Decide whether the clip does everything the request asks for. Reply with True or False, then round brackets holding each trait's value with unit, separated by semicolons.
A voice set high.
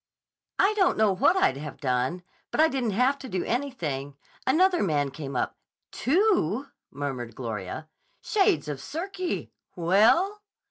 True (200 Hz)